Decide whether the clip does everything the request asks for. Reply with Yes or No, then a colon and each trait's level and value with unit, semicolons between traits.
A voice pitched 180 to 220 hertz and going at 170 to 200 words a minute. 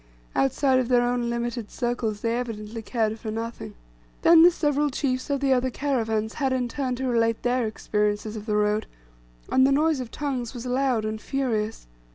No: high, 240 Hz; average, 190 wpm